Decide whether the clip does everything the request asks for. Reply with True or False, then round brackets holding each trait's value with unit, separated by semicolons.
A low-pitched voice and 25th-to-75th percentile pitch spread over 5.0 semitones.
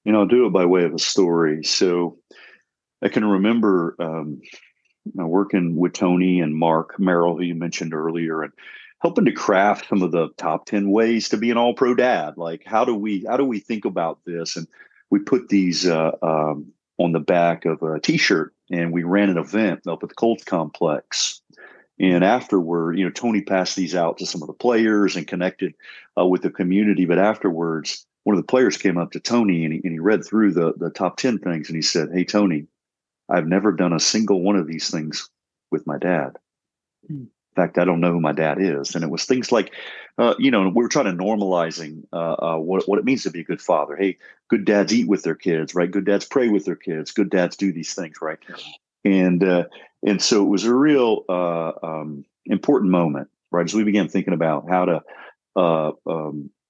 False (90 Hz; 3.3 semitones)